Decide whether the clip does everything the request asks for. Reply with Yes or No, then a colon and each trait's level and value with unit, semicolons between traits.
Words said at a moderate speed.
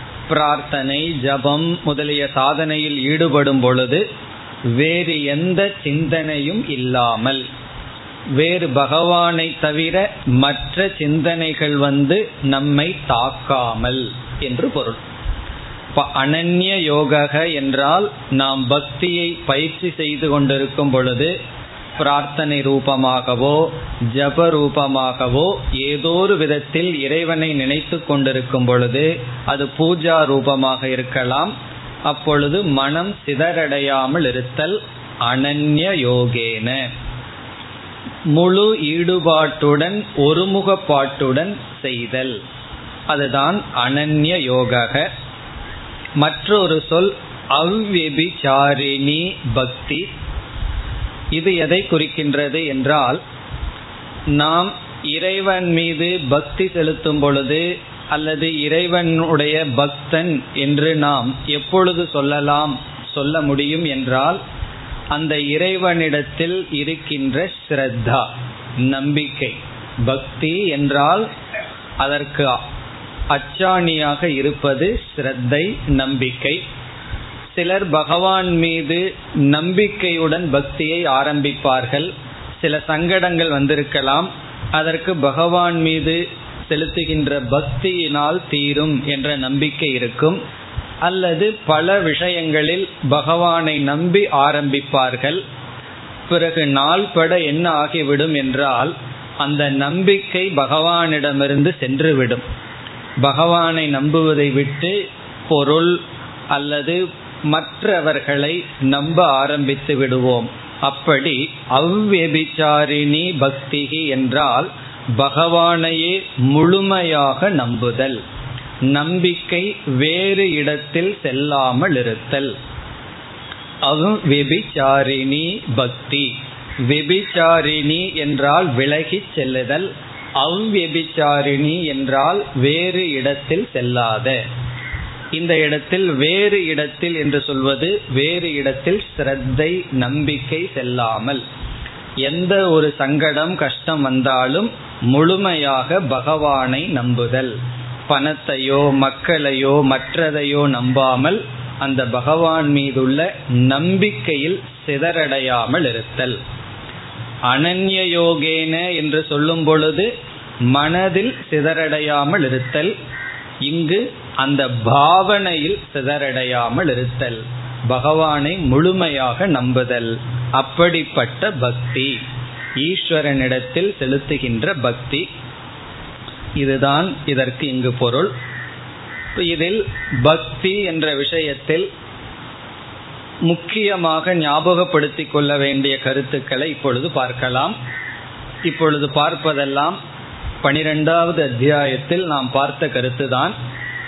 No: slow, 70 wpm